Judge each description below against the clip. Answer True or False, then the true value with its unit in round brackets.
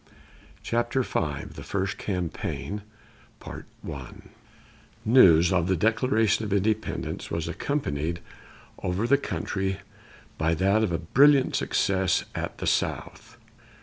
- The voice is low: True (95 Hz)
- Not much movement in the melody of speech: False (4.8 semitones)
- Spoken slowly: True (110 wpm)